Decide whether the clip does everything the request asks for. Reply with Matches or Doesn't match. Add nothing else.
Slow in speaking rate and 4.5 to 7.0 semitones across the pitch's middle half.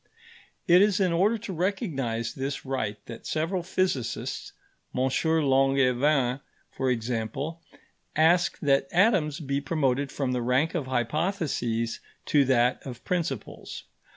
Matches